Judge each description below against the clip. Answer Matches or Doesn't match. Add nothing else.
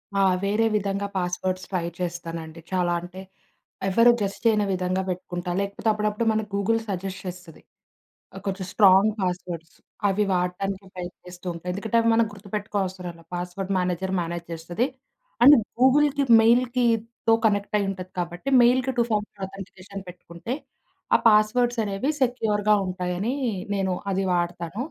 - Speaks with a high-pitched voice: Matches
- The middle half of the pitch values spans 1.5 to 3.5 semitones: Matches